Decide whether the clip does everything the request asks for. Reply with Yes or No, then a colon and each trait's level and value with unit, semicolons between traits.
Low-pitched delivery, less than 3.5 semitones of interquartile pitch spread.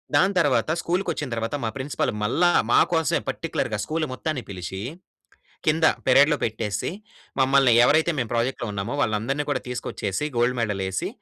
No: low, 130 Hz; wide, 5.5 semitones